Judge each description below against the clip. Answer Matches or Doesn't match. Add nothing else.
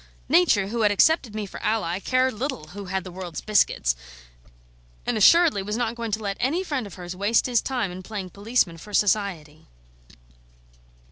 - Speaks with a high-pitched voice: Matches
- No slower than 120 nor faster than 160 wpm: Doesn't match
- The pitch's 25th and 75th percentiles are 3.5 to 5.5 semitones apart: Matches